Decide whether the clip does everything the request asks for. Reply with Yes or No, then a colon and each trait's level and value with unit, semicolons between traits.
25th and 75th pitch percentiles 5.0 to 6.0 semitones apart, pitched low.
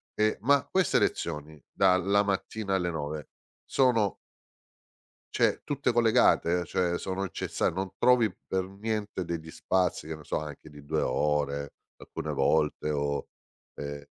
Yes: wide, 5.4 semitones; very low, 90 Hz